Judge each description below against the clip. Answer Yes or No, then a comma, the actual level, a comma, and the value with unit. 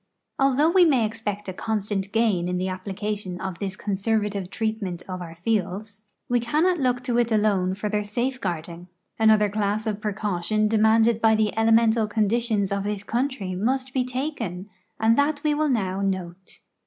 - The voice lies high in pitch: Yes, high, 215 Hz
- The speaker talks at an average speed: Yes, average, 170 wpm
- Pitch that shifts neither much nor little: Yes, average, 3.3 semitones